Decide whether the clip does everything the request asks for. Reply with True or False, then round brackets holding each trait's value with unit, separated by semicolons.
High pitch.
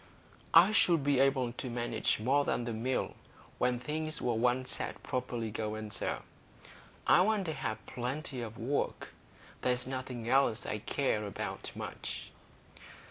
False (125 Hz)